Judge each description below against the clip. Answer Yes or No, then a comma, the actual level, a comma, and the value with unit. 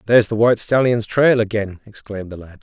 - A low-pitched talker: Yes, low, 110 Hz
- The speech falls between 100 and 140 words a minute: No, fast, 205 wpm